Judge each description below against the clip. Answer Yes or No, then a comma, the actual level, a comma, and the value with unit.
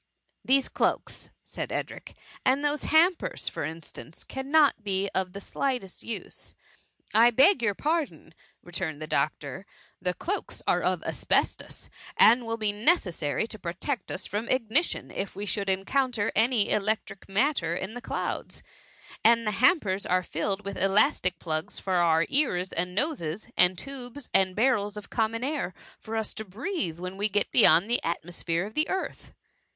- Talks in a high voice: Yes, high, 210 Hz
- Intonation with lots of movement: Yes, wide, 5.9 semitones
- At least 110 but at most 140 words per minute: No, average, 170 wpm